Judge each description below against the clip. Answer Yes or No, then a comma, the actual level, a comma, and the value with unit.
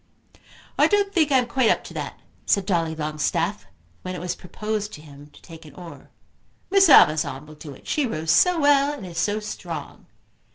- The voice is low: No, medium, 180 Hz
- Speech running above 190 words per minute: Yes, average, 200 wpm